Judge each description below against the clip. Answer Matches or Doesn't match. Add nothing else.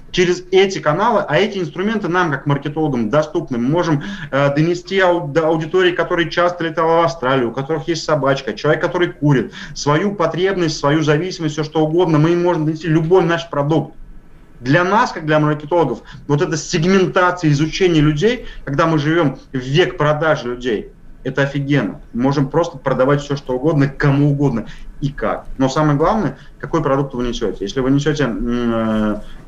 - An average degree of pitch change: Matches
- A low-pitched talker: Doesn't match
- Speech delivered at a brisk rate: Matches